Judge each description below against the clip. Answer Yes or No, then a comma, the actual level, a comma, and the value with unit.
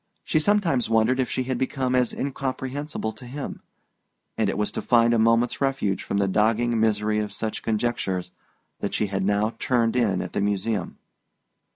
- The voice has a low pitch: Yes, low, 115 Hz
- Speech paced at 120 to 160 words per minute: No, average, 180 wpm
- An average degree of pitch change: Yes, average, 3.5 semitones